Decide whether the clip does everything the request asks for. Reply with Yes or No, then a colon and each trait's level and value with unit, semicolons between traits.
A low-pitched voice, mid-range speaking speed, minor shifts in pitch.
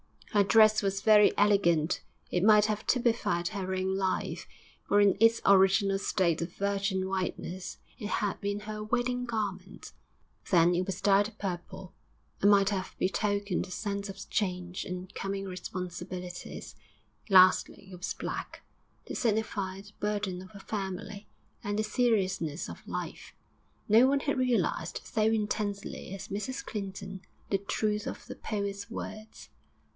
No: high, 200 Hz; average, 145 wpm; narrow, 2.1 semitones